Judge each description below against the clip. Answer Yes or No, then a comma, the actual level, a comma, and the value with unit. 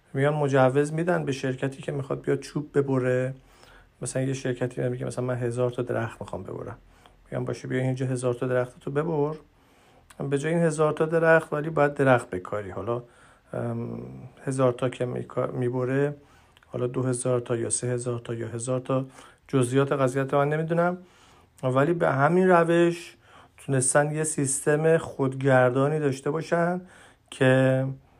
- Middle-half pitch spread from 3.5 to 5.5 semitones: No, average, 2.8 semitones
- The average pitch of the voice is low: Yes, low, 130 Hz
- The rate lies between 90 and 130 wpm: No, fast, 155 wpm